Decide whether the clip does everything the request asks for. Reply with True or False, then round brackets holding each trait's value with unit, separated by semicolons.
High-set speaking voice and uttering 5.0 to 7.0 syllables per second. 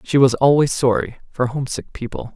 False (130 Hz; 5.6 syllables/s)